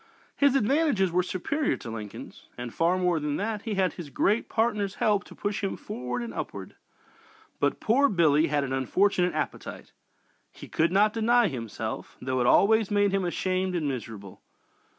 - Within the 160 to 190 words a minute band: Yes, average, 170 wpm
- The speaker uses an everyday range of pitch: No, wide, 6.5 semitones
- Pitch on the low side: No, medium, 185 Hz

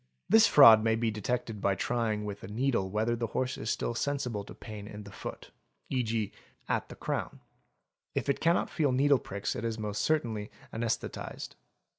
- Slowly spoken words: No, average, 180 wpm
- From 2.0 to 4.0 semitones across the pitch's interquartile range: Yes, average, 3.3 semitones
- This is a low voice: Yes, low, 115 Hz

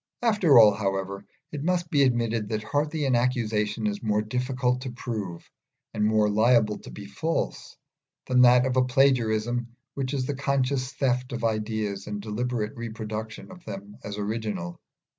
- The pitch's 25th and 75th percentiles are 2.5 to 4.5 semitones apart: Yes, average, 3.3 semitones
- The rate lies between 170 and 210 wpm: No, average, 160 wpm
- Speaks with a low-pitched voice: Yes, low, 115 Hz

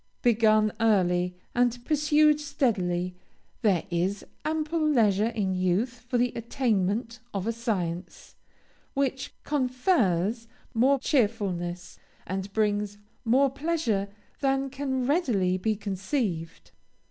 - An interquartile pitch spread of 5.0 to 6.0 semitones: Yes, wide, 5.6 semitones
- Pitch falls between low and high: No, high, 225 Hz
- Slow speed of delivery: Yes, slow, 105 wpm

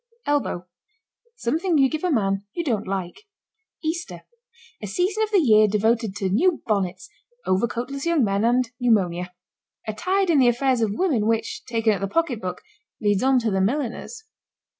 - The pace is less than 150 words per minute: No, average, 165 wpm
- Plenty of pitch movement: Yes, wide, 7.1 semitones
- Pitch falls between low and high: No, high, 235 Hz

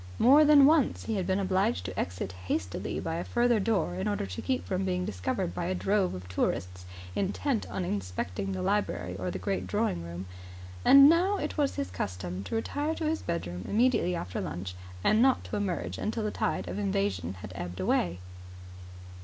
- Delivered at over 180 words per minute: Yes, average, 195 wpm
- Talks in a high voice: No, low, 100 Hz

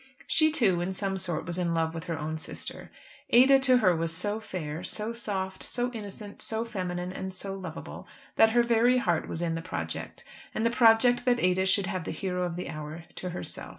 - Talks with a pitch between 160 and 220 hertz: Yes, high, 190 Hz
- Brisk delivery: Yes, fast, 215 wpm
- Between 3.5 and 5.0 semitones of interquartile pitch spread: Yes, average, 4.5 semitones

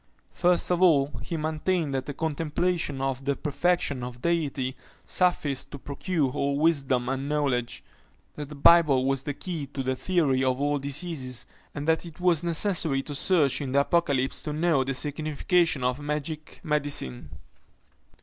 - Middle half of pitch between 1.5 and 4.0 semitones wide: Yes, average, 3.4 semitones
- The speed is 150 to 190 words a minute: Yes, average, 165 wpm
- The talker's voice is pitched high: No, medium, 145 Hz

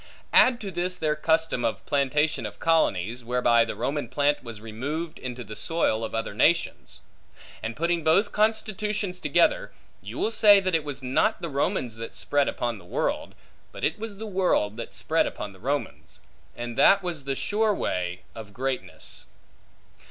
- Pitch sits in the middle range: Yes, medium, 145 Hz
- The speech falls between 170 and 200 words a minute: Yes, average, 175 wpm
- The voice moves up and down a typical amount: No, wide, 7.5 semitones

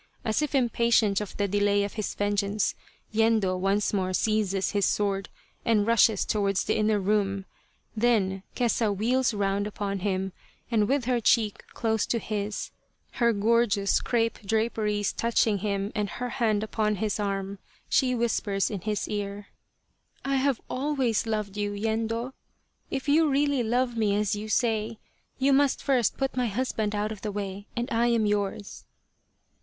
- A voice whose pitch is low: No, high, 215 Hz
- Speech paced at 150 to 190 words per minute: Yes, average, 160 wpm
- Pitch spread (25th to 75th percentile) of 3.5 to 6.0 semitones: No, narrow, 2.6 semitones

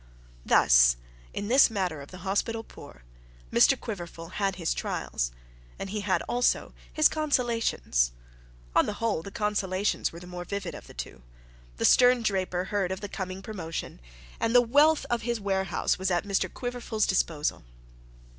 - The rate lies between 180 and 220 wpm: No, average, 165 wpm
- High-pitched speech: Yes, high, 195 Hz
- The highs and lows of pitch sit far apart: No, average, 4.3 semitones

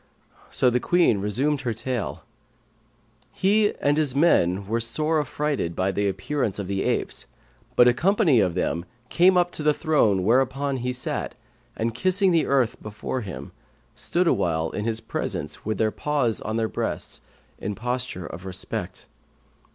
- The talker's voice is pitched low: Yes, low, 125 Hz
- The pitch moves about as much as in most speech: No, wide, 6.4 semitones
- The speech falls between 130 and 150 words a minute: No, average, 160 wpm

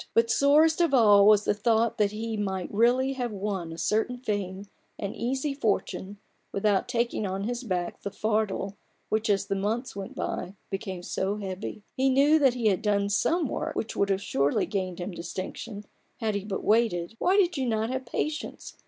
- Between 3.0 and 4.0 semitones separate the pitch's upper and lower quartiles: Yes, average, 3.7 semitones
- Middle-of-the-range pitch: No, high, 210 Hz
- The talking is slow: No, average, 190 wpm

